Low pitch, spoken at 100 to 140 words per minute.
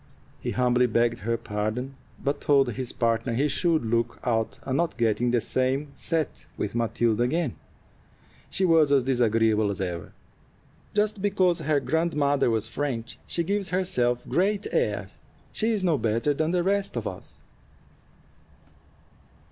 No: low, 130 Hz; average, 150 wpm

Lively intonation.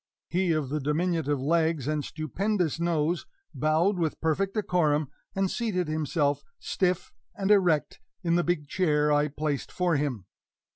No: average, 3.3 semitones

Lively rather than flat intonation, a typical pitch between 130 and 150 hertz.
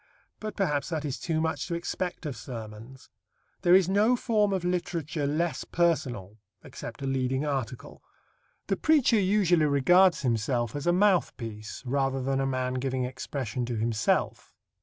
Yes: wide, 5.7 semitones; medium, 140 Hz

